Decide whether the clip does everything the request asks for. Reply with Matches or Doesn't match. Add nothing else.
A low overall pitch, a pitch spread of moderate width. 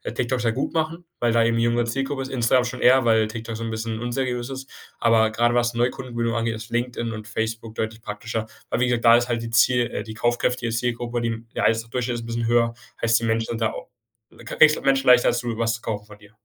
Doesn't match